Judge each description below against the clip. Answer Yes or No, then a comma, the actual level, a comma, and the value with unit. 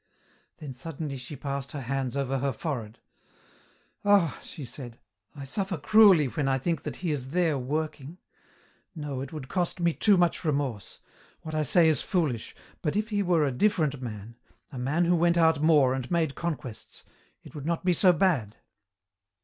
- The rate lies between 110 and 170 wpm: No, average, 180 wpm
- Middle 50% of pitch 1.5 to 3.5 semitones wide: No, average, 4.3 semitones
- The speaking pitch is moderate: Yes, medium, 150 Hz